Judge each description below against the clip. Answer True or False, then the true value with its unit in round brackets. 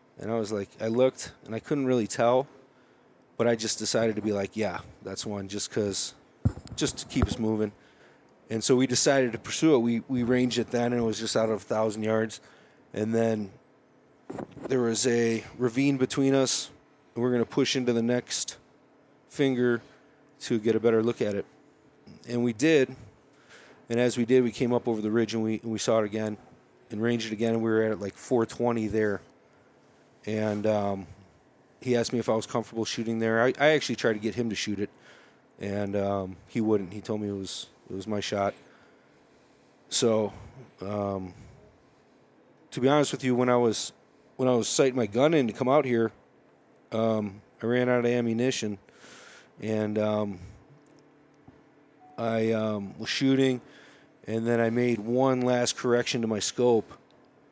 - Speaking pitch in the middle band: False (115 Hz)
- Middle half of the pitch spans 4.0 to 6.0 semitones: False (2.7 semitones)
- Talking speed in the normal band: True (190 wpm)